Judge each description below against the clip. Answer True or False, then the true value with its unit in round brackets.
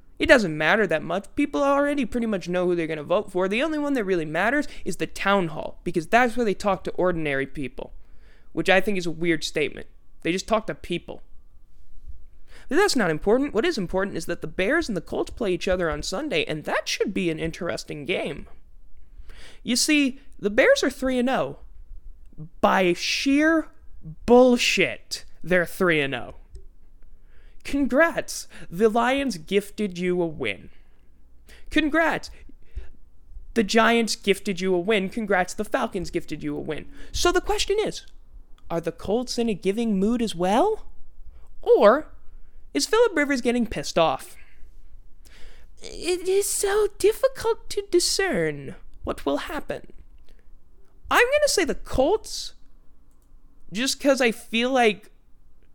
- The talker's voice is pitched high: True (195 Hz)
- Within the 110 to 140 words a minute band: False (155 wpm)